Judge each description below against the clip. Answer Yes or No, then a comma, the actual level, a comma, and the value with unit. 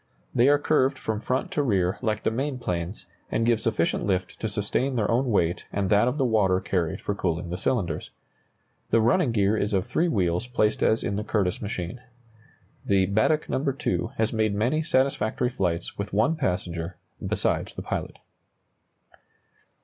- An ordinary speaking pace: Yes, average, 175 wpm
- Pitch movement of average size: Yes, average, 4.8 semitones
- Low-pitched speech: Yes, low, 110 Hz